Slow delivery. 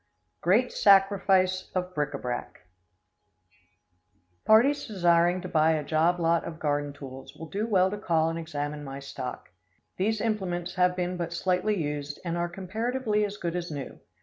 No: average, 165 wpm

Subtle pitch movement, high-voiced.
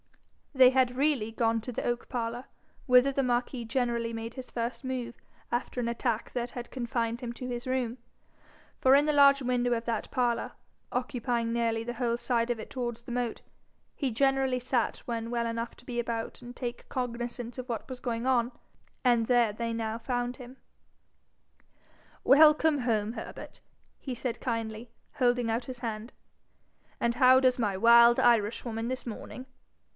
Yes: narrow, 1.6 semitones; high, 240 Hz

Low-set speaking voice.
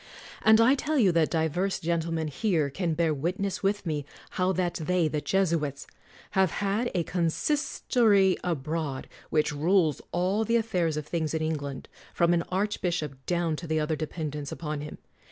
No: medium, 170 Hz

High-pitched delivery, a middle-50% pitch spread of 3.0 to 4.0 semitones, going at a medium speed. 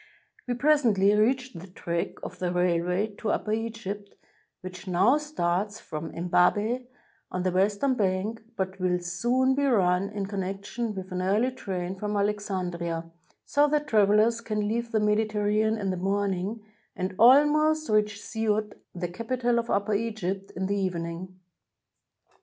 Yes: high, 205 Hz; average, 3.7 semitones; average, 155 wpm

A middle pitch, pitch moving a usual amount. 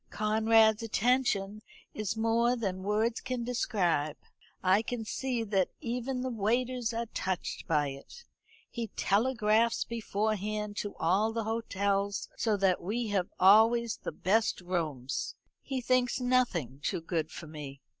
No: high, 215 Hz; average, 3.6 semitones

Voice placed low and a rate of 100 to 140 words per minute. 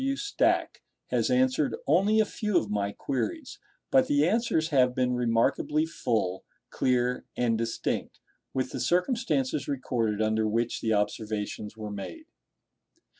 Yes: low, 125 Hz; slow, 135 wpm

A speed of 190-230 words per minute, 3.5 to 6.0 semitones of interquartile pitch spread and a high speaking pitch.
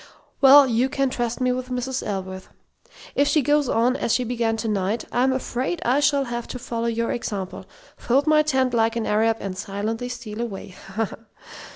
No: average, 195 wpm; average, 2.8 semitones; high, 240 Hz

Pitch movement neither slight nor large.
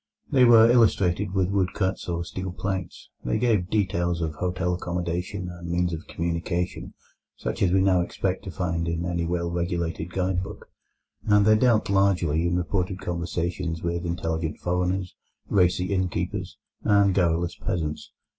No: narrow, 1.9 semitones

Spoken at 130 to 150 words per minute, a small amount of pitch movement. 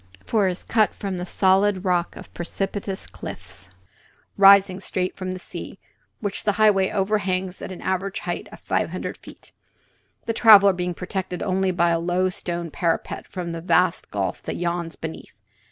No: average, 170 wpm; narrow, 1.9 semitones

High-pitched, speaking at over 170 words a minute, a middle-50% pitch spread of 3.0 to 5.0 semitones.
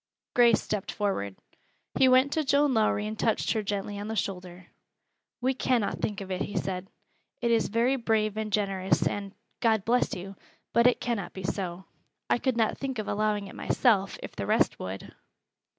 Yes: high, 215 Hz; average, 180 wpm; average, 3.3 semitones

